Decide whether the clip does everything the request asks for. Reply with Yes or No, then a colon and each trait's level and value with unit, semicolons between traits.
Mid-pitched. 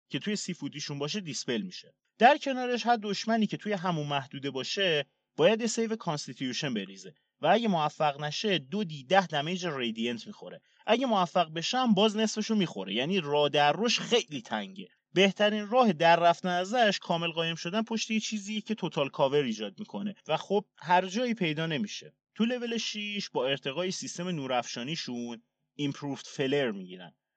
Yes: medium, 180 Hz